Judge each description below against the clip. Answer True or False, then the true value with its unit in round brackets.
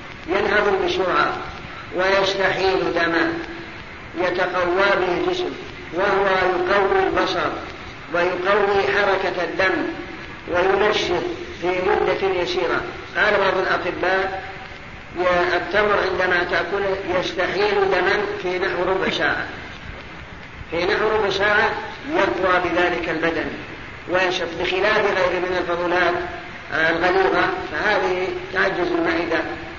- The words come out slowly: False (90 wpm)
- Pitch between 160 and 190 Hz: True (185 Hz)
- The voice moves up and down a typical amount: False (2.1 semitones)